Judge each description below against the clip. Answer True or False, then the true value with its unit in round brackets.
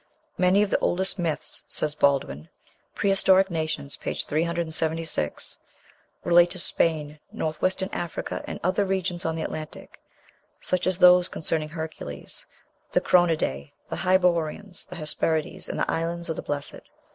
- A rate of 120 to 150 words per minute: True (140 wpm)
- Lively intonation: False (2.8 semitones)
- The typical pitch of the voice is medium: True (165 Hz)